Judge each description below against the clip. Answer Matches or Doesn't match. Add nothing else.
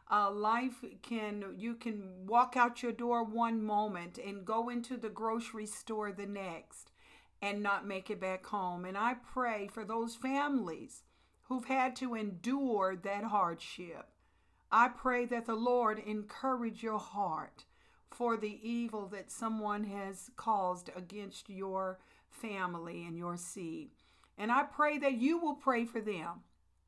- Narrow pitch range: Doesn't match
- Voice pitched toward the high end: Matches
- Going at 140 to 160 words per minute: Matches